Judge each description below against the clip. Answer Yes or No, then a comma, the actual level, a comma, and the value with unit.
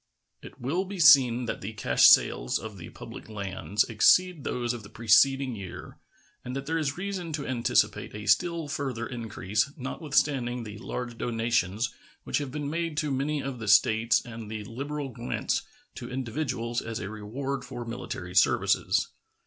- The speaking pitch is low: Yes, low, 120 Hz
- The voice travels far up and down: No, average, 4.2 semitones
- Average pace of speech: Yes, average, 165 wpm